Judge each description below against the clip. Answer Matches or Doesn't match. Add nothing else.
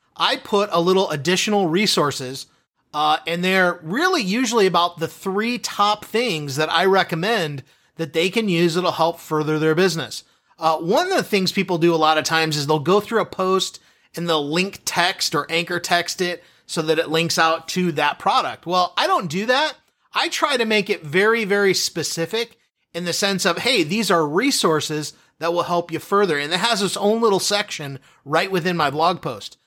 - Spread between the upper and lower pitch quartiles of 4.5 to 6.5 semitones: Doesn't match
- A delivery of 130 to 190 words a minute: Doesn't match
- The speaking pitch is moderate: Matches